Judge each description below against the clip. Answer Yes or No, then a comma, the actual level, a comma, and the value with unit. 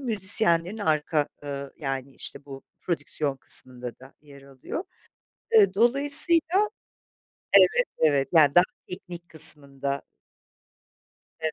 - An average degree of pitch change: No, wide, 6.6 semitones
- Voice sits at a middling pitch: Yes, medium, 155 Hz